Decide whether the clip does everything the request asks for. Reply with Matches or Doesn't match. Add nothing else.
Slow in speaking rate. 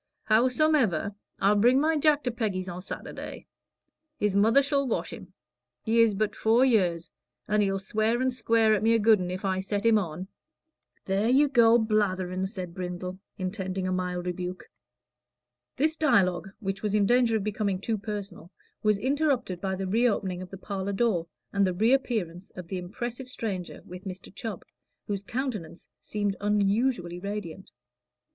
Doesn't match